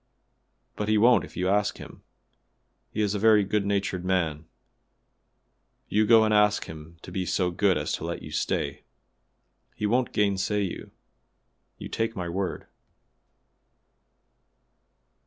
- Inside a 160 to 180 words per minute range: No, average, 140 wpm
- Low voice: Yes, low, 100 Hz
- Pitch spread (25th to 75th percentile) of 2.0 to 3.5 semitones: Yes, narrow, 2.5 semitones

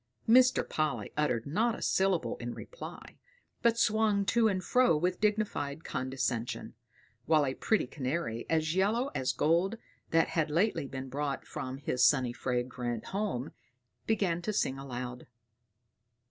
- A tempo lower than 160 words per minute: Yes, average, 140 wpm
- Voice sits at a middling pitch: Yes, medium, 155 Hz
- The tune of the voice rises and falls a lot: Yes, wide, 7.8 semitones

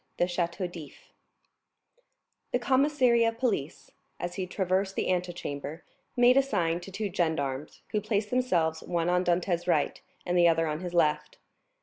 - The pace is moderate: Yes, average, 155 wpm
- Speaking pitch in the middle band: Yes, medium, 180 Hz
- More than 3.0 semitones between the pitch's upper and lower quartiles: Yes, average, 4.0 semitones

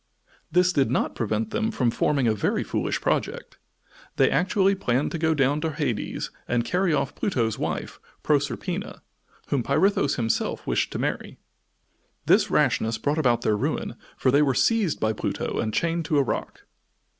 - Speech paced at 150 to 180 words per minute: Yes, average, 170 wpm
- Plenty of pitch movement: Yes, wide, 6.0 semitones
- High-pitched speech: No, medium, 140 Hz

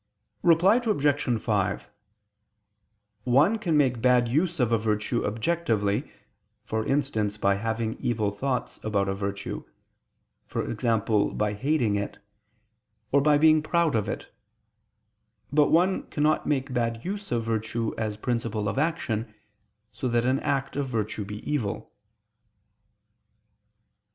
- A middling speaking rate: No, slow, 125 wpm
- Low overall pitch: Yes, low, 120 Hz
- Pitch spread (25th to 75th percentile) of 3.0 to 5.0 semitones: No, wide, 5.5 semitones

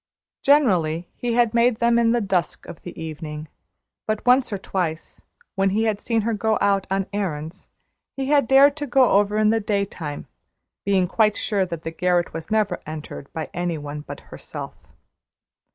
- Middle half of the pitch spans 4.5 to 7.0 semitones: Yes, average, 5.2 semitones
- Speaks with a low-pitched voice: No, high, 200 Hz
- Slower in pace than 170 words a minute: No, average, 180 wpm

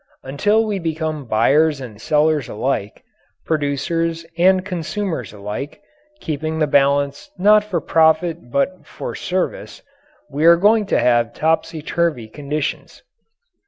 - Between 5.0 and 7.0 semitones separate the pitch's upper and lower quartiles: No, average, 3.6 semitones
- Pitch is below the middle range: No, medium, 155 Hz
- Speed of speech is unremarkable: No, slow, 125 wpm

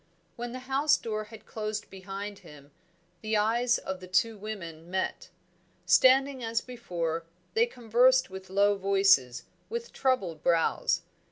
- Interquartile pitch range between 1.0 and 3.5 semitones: No, average, 4.6 semitones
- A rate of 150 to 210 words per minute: No, average, 140 wpm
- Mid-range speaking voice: No, high, 210 Hz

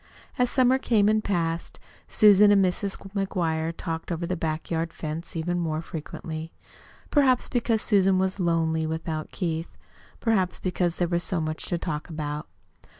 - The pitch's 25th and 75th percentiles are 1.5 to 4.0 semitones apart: Yes, average, 3.6 semitones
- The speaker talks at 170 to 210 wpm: No, average, 160 wpm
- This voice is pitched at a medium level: Yes, medium, 175 Hz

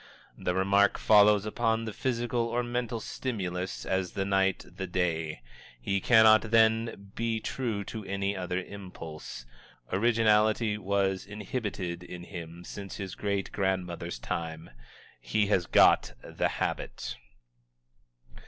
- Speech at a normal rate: No, slow, 125 wpm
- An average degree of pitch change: Yes, average, 3.4 semitones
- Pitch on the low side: Yes, low, 100 Hz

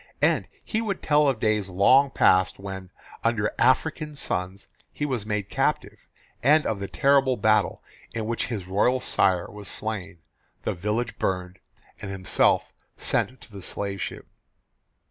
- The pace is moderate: Yes, average, 150 wpm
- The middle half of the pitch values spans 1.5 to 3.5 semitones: No, average, 4.9 semitones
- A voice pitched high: No, low, 105 Hz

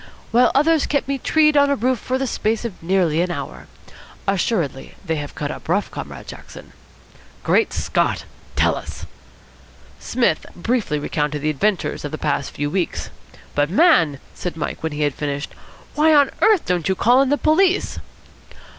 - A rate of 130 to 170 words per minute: No, average, 180 wpm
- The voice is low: No, high, 190 Hz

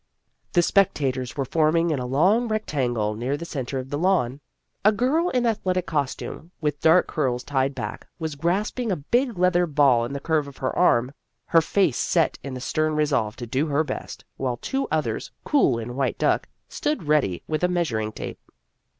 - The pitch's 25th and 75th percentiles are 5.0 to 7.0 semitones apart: Yes, wide, 5.5 semitones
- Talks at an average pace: Yes, average, 190 wpm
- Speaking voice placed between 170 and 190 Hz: No, medium, 150 Hz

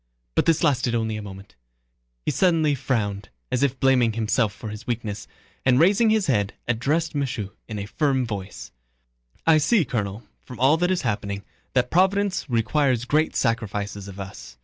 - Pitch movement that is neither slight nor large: No, wide, 6.4 semitones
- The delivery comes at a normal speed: Yes, average, 170 wpm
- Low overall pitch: Yes, low, 120 Hz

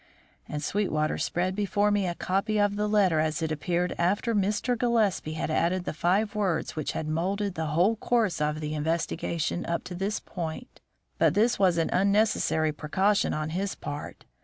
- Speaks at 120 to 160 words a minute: No, average, 180 wpm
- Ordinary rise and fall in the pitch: Yes, average, 4.4 semitones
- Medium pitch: Yes, medium, 180 Hz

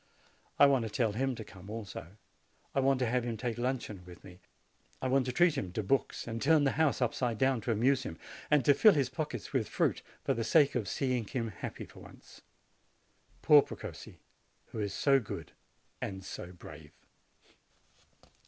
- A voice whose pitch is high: No, low, 120 Hz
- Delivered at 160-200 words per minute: Yes, average, 190 wpm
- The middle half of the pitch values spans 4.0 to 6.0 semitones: Yes, average, 4.4 semitones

